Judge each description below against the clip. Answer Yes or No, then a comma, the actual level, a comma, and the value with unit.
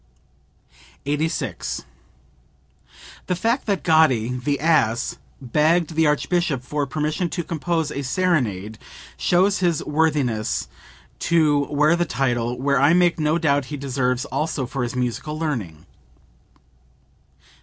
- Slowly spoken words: Yes, slow, 120 wpm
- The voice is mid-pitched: Yes, medium, 150 Hz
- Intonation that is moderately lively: Yes, average, 4.5 semitones